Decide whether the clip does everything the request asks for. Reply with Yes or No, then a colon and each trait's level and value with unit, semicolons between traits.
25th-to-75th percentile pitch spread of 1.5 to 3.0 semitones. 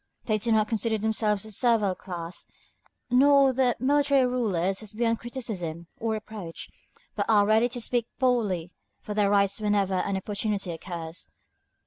No: average, 3.5 semitones